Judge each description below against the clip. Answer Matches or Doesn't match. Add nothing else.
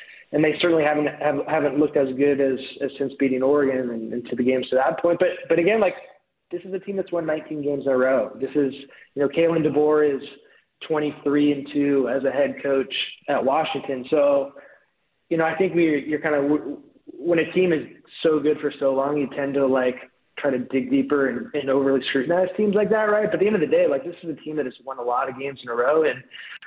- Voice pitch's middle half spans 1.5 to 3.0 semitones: Doesn't match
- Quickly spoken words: Matches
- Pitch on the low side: Doesn't match